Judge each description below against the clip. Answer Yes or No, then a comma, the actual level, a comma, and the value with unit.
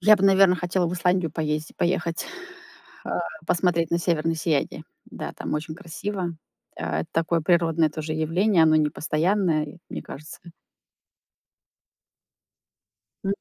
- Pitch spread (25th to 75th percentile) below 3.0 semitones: Yes, narrow, 2.4 semitones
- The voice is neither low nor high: Yes, medium, 165 Hz